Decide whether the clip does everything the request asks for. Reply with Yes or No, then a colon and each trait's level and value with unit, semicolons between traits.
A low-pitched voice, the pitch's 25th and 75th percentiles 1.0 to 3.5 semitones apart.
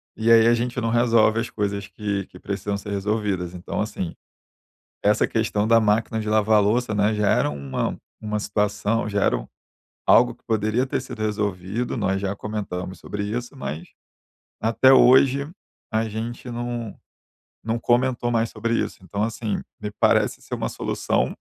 Yes: low, 110 Hz; narrow, 2.4 semitones